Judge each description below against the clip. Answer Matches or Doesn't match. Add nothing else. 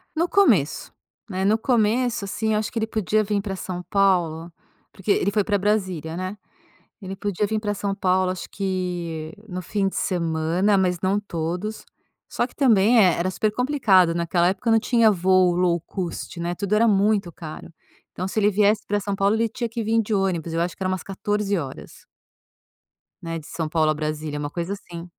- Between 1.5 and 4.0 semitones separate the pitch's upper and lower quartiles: Matches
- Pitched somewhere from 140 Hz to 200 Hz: Matches